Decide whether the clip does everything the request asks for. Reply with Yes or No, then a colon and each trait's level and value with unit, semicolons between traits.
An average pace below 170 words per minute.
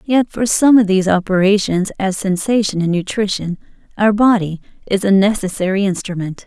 Yes: average, 150 wpm